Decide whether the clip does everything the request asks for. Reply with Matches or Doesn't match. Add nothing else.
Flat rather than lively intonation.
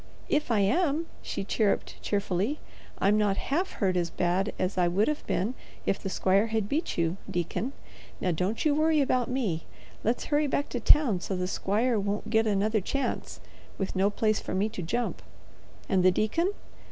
Doesn't match